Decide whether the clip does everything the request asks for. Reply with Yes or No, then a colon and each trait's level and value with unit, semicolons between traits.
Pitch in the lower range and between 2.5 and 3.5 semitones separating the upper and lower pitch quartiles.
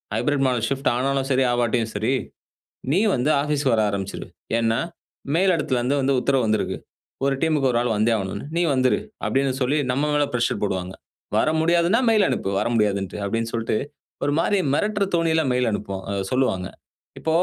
No: low, 130 Hz; average, 4.9 semitones